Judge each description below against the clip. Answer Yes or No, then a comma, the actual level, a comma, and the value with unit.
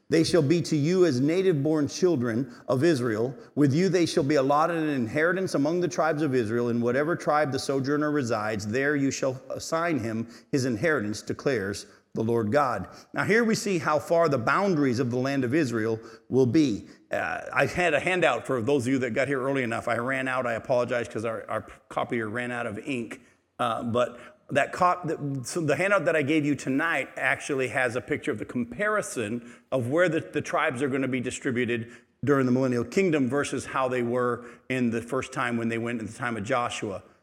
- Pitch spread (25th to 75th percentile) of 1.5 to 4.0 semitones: No, average, 4.4 semitones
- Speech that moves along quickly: Yes, fast, 210 wpm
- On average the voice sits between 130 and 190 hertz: Yes, low, 135 Hz